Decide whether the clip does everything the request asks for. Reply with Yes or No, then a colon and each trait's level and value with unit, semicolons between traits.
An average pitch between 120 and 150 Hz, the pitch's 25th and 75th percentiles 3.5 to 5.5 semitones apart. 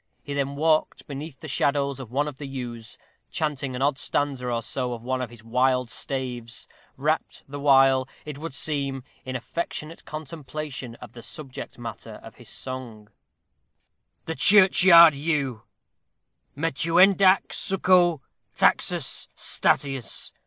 No: medium, 140 Hz; average, 3.1 semitones